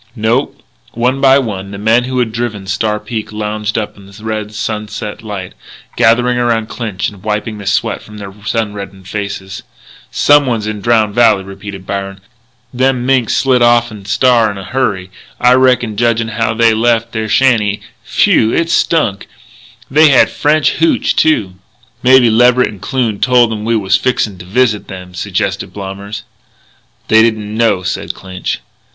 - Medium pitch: No, low, 110 Hz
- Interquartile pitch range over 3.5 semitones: No, average, 3.0 semitones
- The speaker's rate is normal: Yes, average, 160 wpm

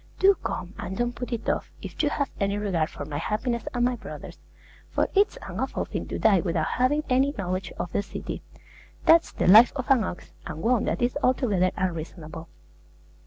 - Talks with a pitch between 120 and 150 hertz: No, high, 215 Hz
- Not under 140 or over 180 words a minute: No, average, 200 wpm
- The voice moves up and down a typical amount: No, wide, 5.9 semitones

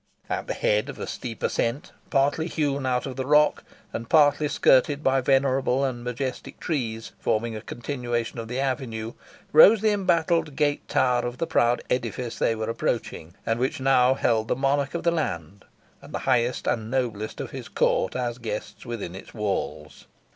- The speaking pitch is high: No, low, 125 Hz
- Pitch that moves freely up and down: No, average, 3.5 semitones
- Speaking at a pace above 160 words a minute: Yes, average, 180 wpm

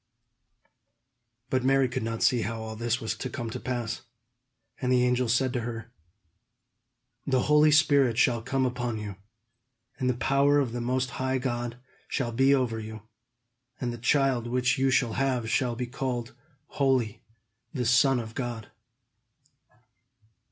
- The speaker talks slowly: No, average, 155 wpm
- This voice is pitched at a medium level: No, low, 125 Hz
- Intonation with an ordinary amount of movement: No, narrow, 2.1 semitones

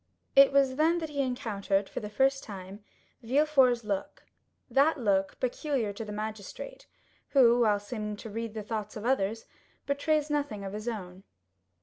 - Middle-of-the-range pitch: No, high, 230 Hz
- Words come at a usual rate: Yes, average, 155 wpm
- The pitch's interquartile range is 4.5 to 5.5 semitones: Yes, average, 4.8 semitones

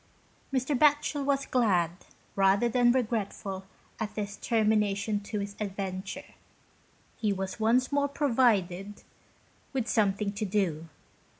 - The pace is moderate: No, slow, 115 wpm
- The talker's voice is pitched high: Yes, high, 210 Hz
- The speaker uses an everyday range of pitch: Yes, average, 4.0 semitones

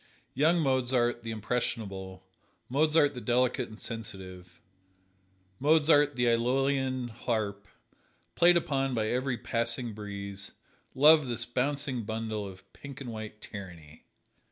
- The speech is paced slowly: Yes, slow, 115 wpm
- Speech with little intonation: No, average, 4.2 semitones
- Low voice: Yes, low, 120 Hz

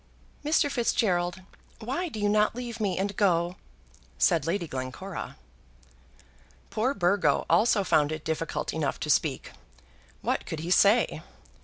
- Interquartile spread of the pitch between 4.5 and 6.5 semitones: Yes, average, 4.8 semitones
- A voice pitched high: Yes, high, 195 Hz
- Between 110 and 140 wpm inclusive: Yes, slow, 135 wpm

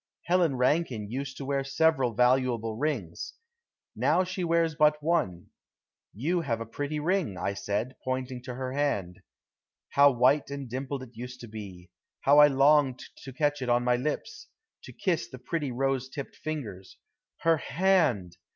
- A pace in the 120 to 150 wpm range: No, average, 160 wpm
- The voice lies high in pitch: No, low, 135 Hz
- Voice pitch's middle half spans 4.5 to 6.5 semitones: No, average, 3.8 semitones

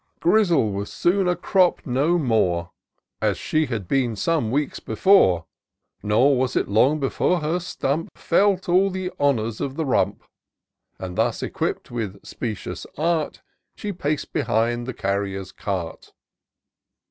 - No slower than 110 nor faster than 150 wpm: Yes, average, 140 wpm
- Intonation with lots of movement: Yes, wide, 8.0 semitones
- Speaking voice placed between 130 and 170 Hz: Yes, low, 135 Hz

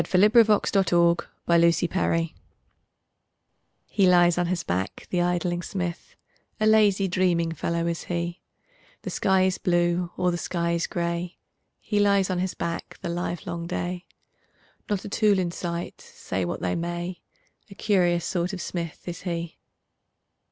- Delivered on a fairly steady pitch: Yes, narrow, 1.6 semitones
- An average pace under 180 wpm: Yes, average, 155 wpm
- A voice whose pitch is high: No, medium, 175 Hz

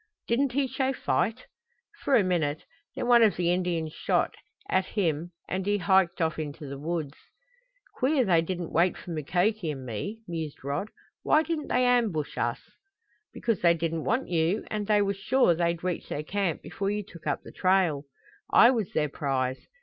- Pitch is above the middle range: No, medium, 180 Hz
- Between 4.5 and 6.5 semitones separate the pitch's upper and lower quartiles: Yes, average, 5.2 semitones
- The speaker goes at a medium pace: Yes, average, 180 wpm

